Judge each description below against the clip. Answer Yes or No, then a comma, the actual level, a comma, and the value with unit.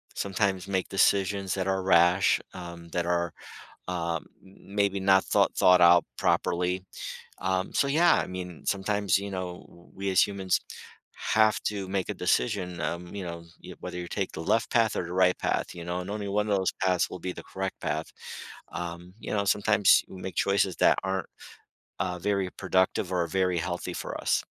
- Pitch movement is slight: Yes, narrow, 1.9 semitones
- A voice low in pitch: Yes, very low, 95 Hz